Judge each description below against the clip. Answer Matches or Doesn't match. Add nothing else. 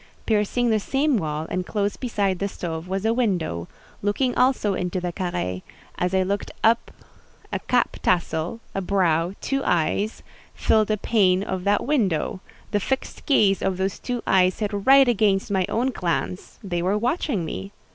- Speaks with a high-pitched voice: Matches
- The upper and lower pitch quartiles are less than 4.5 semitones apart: Matches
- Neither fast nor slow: Matches